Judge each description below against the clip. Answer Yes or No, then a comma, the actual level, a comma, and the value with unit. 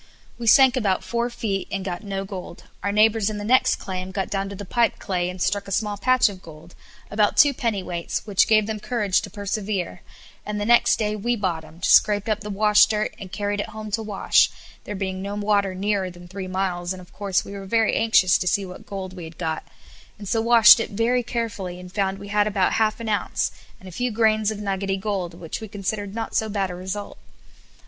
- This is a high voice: Yes, high, 200 Hz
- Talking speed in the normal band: No, fast, 225 wpm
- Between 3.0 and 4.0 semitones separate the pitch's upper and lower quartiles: No, narrow, 2.4 semitones